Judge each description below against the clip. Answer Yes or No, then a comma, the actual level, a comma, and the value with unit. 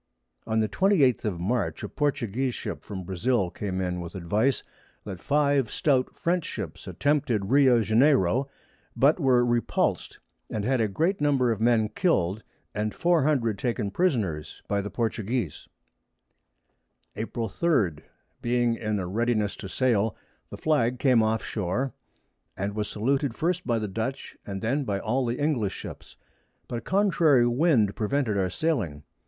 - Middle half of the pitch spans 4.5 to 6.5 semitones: Yes, average, 5.0 semitones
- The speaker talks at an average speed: Yes, average, 150 wpm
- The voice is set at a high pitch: No, low, 115 Hz